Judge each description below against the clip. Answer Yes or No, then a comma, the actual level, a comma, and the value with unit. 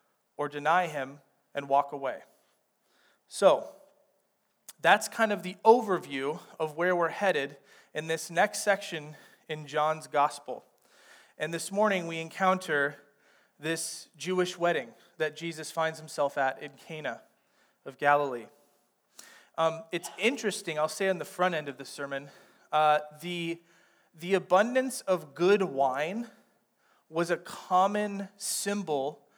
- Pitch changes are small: No, average, 4.3 semitones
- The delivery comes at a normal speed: No, slow, 130 wpm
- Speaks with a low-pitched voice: No, medium, 165 Hz